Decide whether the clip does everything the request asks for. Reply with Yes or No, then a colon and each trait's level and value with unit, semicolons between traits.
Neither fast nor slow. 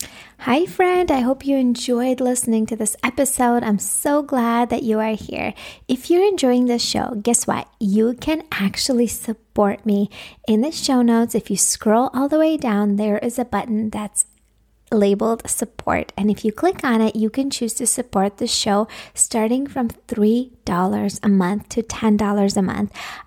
Yes: average, 180 wpm